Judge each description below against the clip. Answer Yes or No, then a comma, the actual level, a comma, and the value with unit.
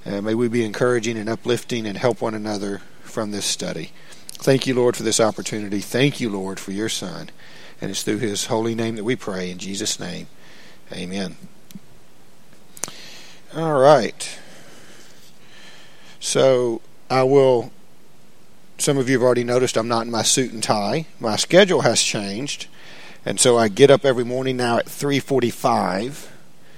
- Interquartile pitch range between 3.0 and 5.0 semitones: Yes, average, 3.5 semitones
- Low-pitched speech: Yes, low, 120 Hz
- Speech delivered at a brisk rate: No, average, 160 wpm